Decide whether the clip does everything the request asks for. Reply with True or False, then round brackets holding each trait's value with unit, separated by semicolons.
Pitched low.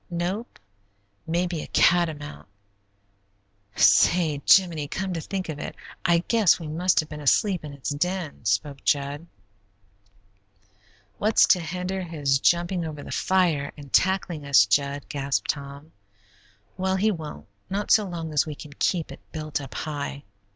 False (160 Hz)